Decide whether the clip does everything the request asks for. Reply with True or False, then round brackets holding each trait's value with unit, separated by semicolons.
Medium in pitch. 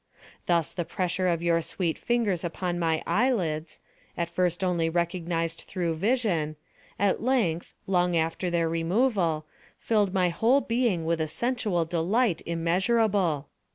True (175 Hz)